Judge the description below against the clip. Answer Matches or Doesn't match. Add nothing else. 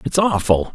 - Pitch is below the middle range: Matches